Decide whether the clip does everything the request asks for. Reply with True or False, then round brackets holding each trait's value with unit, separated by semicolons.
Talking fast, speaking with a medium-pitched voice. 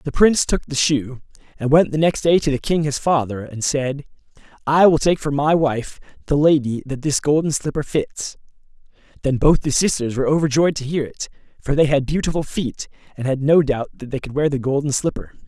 True (215 wpm; 145 Hz)